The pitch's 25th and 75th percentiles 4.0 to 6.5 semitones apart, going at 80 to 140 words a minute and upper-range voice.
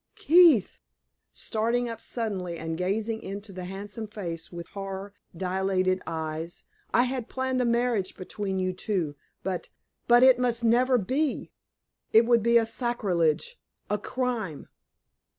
Yes: average, 4.5 semitones; slow, 135 wpm; high, 210 Hz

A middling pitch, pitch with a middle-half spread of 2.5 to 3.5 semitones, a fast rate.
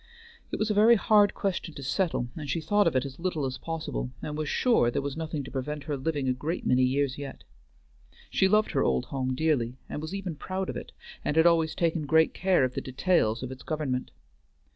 No: medium, 150 Hz; average, 4.7 semitones; fast, 230 wpm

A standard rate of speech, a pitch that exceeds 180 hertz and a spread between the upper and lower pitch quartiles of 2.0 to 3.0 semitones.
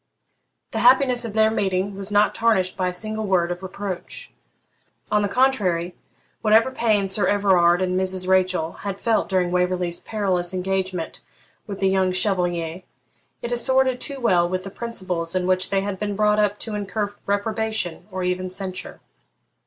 Yes: average, 165 wpm; high, 190 Hz; narrow, 2.6 semitones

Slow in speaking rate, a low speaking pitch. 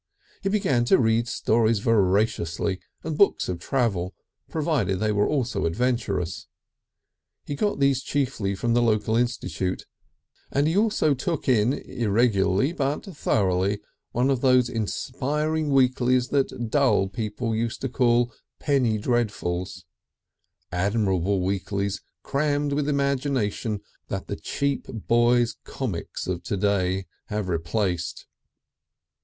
Yes: slow, 120 wpm; low, 115 Hz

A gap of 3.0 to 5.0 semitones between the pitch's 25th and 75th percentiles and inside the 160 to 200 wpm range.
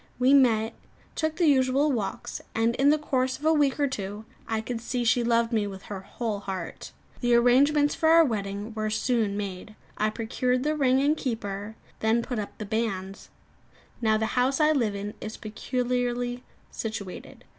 Yes: average, 3.4 semitones; average, 180 wpm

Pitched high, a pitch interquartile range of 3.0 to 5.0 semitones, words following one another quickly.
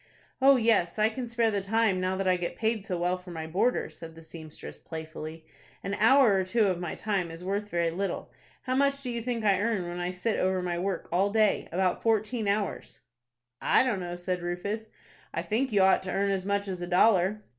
Yes: high, 195 Hz; average, 3.8 semitones; fast, 220 wpm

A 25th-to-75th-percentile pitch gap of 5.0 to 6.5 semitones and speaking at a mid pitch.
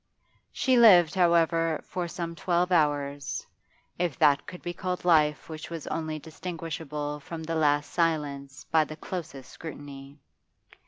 No: average, 2.7 semitones; medium, 160 Hz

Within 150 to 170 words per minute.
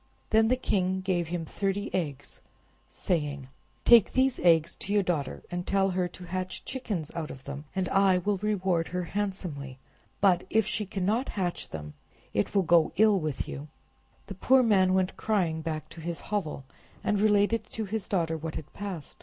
No: average, 180 wpm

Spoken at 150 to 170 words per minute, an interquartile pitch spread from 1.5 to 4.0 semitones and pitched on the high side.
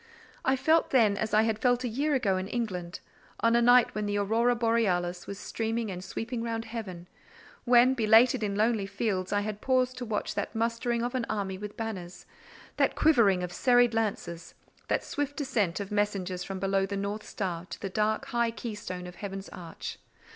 No: average, 185 wpm; average, 3.5 semitones; high, 215 Hz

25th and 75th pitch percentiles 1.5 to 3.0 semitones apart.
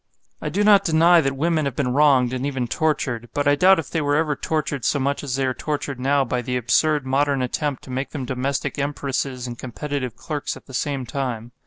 Yes: narrow, 2.6 semitones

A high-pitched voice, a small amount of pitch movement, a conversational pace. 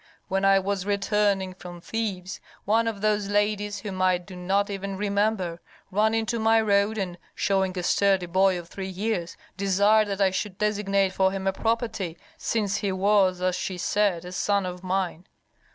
Yes: high, 195 Hz; narrow, 1.9 semitones; average, 180 wpm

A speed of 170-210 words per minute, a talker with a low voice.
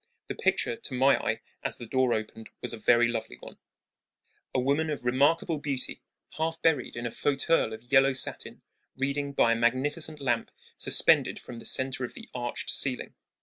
Yes: average, 180 wpm; low, 130 Hz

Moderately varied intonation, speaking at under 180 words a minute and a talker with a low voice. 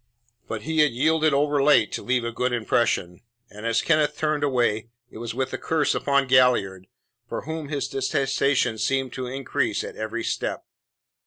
Yes: average, 3.8 semitones; average, 170 wpm; low, 130 Hz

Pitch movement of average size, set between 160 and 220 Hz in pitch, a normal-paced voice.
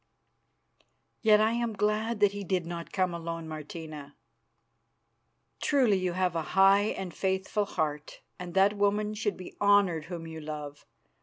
Yes: average, 3.8 semitones; high, 190 Hz; average, 150 wpm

